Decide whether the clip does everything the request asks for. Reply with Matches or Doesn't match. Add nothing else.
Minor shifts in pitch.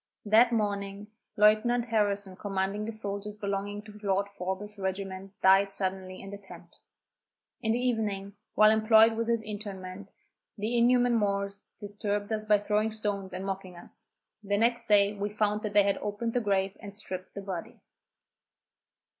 Matches